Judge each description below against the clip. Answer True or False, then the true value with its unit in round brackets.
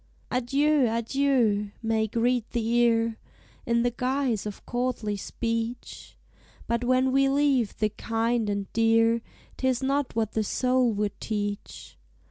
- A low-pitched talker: False (235 Hz)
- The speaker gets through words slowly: True (130 wpm)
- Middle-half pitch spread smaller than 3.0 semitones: True (2.4 semitones)